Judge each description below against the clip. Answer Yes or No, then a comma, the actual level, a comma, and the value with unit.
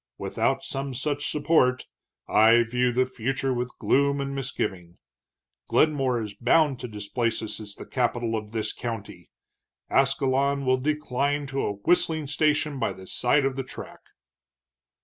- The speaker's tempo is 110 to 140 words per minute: No, average, 150 wpm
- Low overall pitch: Yes, low, 130 Hz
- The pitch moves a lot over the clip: No, average, 3.4 semitones